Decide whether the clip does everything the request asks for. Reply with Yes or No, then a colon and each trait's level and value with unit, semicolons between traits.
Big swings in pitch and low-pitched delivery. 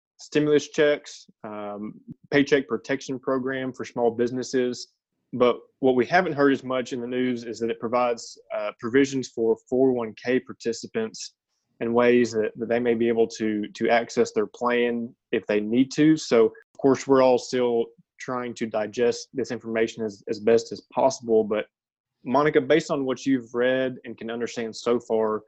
No: average, 2.8 semitones; low, 120 Hz